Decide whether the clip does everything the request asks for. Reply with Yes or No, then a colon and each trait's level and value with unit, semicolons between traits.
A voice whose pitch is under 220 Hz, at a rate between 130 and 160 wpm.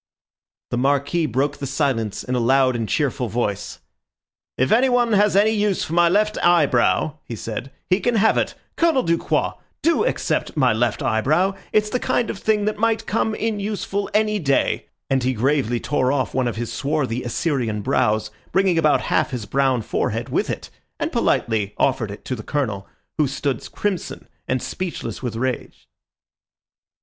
No: medium, 140 Hz; average, 175 wpm